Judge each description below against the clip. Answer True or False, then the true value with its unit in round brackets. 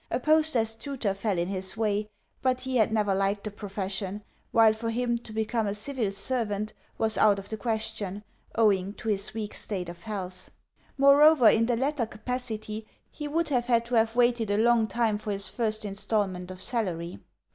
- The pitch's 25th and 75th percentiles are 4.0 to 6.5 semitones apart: False (2.9 semitones)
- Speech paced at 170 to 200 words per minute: True (190 wpm)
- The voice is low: False (220 Hz)